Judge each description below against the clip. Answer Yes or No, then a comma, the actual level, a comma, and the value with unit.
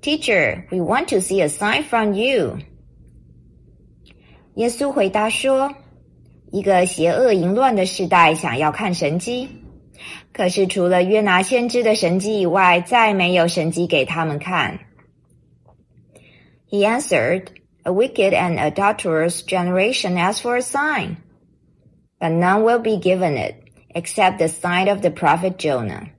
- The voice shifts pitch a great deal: No, average, 4.2 semitones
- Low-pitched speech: No, medium, 185 Hz